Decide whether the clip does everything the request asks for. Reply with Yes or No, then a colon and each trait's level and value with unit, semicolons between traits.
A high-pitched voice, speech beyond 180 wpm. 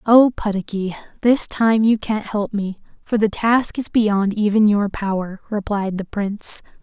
No: high, 210 Hz; average, 165 wpm